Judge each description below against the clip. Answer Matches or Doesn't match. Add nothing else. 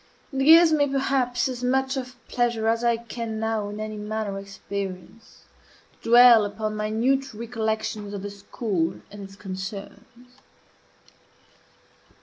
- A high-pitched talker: Matches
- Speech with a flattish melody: Doesn't match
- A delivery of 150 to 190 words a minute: Doesn't match